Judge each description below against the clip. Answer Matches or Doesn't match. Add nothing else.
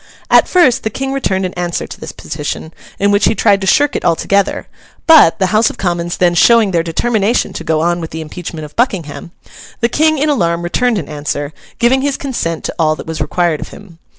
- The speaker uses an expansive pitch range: Matches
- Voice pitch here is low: Doesn't match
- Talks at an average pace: Doesn't match